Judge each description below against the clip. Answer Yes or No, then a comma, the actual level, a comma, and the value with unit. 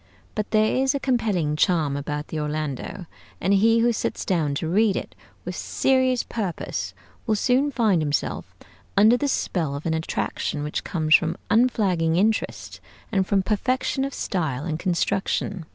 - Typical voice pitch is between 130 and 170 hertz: No, high, 190 Hz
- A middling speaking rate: Yes, average, 160 wpm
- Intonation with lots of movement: Yes, wide, 6.2 semitones